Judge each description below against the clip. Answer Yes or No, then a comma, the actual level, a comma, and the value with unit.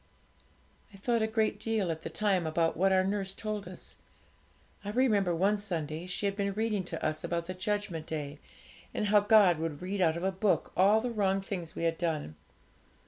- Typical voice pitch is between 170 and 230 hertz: Yes, high, 190 Hz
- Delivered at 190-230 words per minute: Yes, average, 200 wpm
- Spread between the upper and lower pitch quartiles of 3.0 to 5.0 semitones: Yes, average, 3.7 semitones